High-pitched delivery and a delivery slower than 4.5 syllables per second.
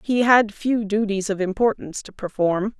No: high, 210 Hz; 4.8 syllables/s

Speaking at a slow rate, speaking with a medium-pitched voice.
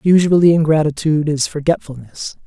Yes: slow, 100 wpm; medium, 155 Hz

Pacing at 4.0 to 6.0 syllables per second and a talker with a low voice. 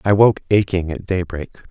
Yes: 4.7 syllables/s; very low, 95 Hz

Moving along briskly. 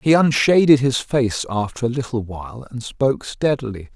No: average, 165 wpm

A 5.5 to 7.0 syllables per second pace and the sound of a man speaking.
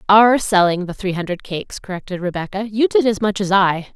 No: 5.7 syllables/s; female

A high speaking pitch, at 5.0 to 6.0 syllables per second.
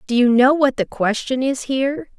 Yes: very high, 260 Hz; 5.1 syllables/s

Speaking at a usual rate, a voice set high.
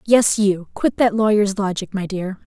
Yes: average, 190 wpm; high, 205 Hz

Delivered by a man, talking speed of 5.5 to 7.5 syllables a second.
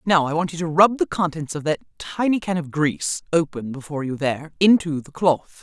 No: female; 5.7 syllables/s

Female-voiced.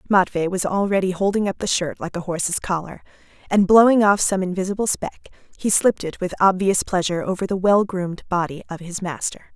Yes: female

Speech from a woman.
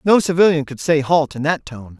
No: male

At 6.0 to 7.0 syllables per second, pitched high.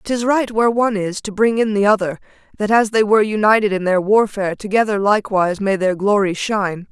Yes: 6.1 syllables/s; high, 205 Hz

